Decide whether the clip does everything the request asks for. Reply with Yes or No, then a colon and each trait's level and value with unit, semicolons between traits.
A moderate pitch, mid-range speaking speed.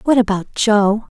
No: high, 215 Hz; average, 150 wpm